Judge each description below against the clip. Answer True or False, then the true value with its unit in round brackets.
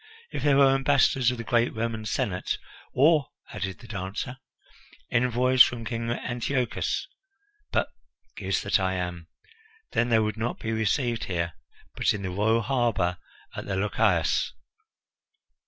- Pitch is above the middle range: False (115 Hz)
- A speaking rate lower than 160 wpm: True (145 wpm)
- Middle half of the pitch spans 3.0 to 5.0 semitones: True (4.0 semitones)